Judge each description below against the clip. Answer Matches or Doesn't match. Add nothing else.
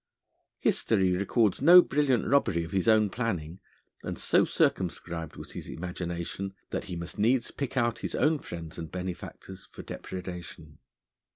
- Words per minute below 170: Matches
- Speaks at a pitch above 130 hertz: Doesn't match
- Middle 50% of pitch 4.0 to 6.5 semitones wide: Matches